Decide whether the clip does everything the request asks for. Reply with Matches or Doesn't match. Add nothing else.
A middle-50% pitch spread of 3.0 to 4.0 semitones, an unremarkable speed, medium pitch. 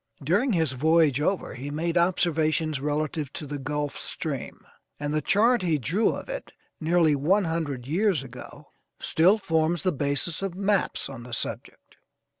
Matches